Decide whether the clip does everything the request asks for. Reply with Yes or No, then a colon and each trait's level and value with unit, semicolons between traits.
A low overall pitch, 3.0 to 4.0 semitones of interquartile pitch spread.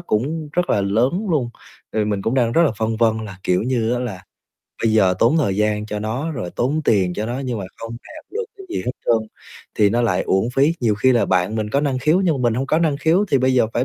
No: low, 120 Hz; average, 4.9 semitones